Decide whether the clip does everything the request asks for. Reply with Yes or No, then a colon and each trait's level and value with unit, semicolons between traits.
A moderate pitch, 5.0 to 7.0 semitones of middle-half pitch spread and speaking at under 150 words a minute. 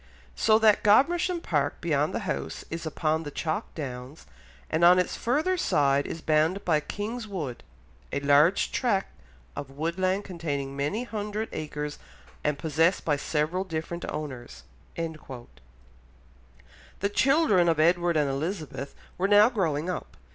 Yes: medium, 160 Hz; wide, 5.6 semitones; average, 140 wpm